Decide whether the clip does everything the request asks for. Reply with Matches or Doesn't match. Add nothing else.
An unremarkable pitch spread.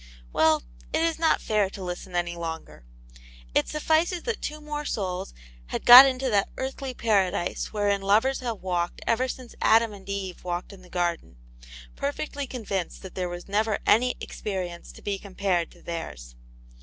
Doesn't match